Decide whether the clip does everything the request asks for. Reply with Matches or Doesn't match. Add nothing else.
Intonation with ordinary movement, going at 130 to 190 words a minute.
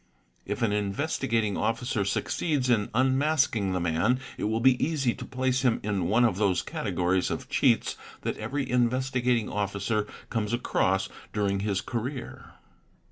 Matches